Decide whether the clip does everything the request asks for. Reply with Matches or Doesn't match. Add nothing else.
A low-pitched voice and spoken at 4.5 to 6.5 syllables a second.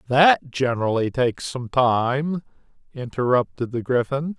Doesn't match